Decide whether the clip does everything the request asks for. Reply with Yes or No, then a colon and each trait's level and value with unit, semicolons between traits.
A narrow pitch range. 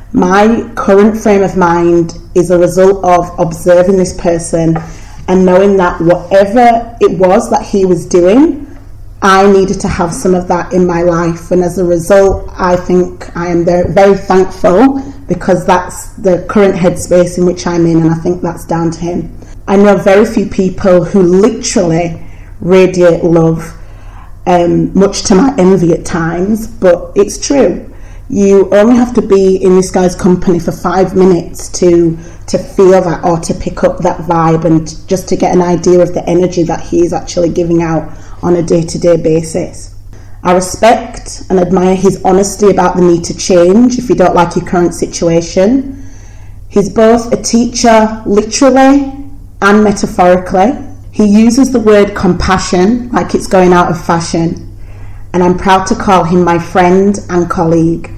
Yes: narrow, 2.3 semitones